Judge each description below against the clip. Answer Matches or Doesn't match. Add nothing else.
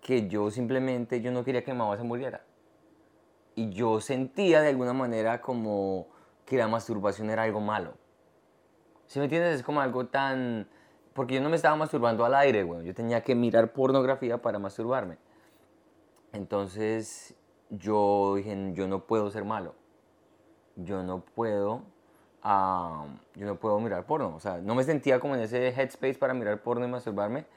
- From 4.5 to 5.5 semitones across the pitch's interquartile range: Doesn't match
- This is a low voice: Matches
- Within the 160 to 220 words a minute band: Matches